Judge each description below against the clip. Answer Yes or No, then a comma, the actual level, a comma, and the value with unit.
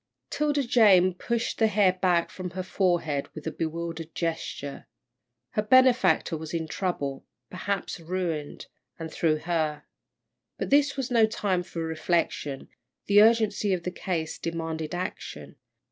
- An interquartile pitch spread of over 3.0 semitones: Yes, average, 4.2 semitones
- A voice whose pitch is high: No, medium, 175 Hz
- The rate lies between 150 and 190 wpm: No, average, 140 wpm